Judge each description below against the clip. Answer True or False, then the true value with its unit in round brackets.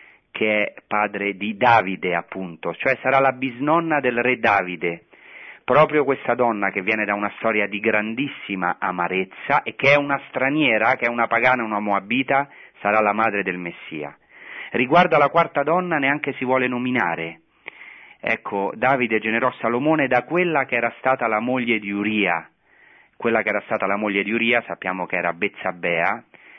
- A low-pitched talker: True (115 Hz)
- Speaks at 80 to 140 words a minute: False (165 wpm)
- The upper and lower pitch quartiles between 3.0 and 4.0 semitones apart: False (4.6 semitones)